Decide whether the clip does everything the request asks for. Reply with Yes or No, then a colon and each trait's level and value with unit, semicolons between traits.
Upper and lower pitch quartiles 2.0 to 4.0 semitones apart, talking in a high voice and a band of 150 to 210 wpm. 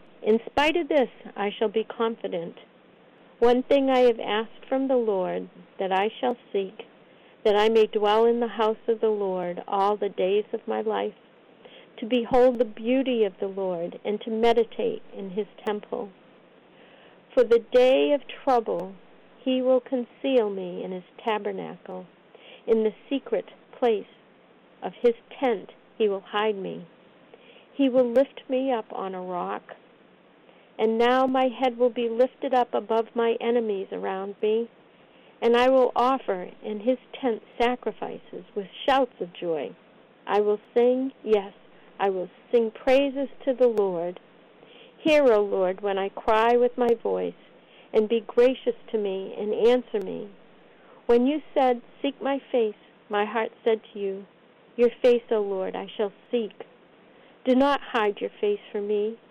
Yes: average, 3.4 semitones; high, 230 Hz; average, 160 wpm